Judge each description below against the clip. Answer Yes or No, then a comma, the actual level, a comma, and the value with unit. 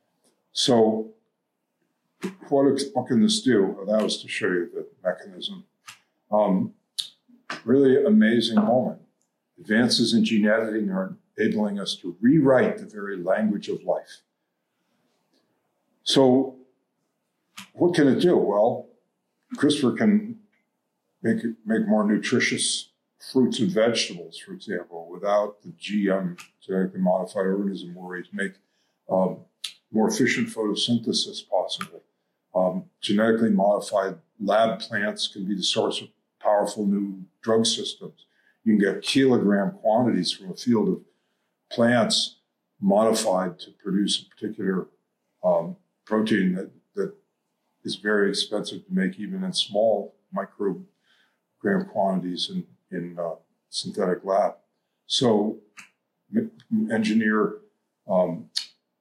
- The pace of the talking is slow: Yes, slow, 120 wpm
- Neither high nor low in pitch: No, low, 115 Hz